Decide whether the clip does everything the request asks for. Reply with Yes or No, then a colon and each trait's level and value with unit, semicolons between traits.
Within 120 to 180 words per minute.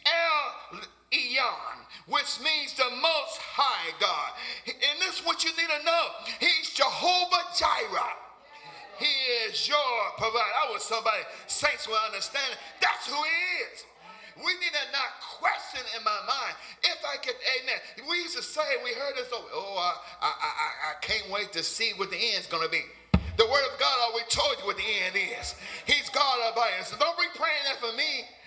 No: average, 190 wpm